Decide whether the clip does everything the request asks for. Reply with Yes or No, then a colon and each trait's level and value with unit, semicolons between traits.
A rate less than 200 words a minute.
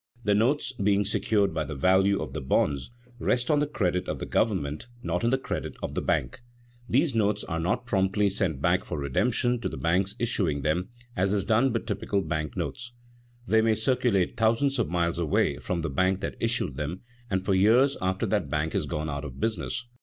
No: fast, 205 wpm